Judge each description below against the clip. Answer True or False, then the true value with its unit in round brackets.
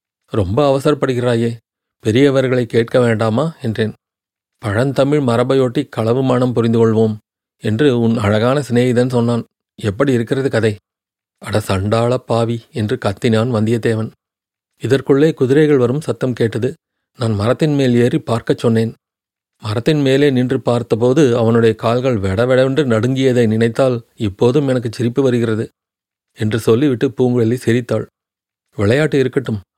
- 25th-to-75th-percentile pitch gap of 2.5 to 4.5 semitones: True (2.8 semitones)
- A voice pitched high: False (120 Hz)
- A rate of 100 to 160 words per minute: True (115 wpm)